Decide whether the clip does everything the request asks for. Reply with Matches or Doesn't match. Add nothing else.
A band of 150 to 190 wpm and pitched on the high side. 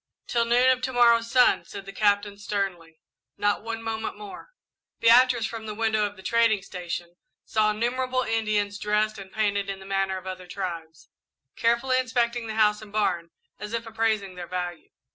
Matches